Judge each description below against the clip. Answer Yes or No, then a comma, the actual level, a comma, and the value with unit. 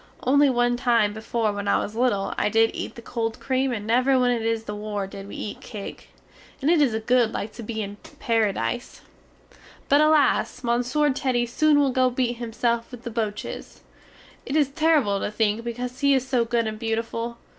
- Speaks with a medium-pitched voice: No, high, 235 Hz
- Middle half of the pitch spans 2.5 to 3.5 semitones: Yes, average, 2.8 semitones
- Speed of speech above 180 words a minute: Yes, average, 200 wpm